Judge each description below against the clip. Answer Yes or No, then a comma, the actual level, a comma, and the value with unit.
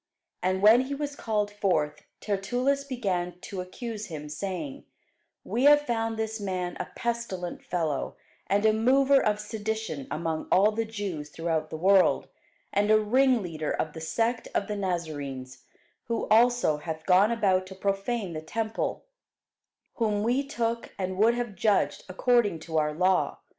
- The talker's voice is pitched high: Yes, high, 205 Hz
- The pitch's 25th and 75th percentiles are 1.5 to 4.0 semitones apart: No, average, 4.7 semitones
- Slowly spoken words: No, average, 155 wpm